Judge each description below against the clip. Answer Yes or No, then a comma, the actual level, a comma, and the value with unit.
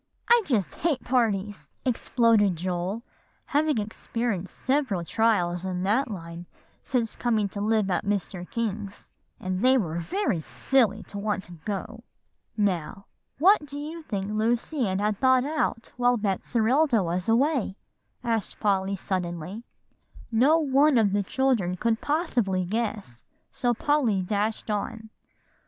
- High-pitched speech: Yes, high, 215 Hz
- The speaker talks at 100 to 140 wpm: Yes, slow, 135 wpm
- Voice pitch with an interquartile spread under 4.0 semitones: No, average, 4.7 semitones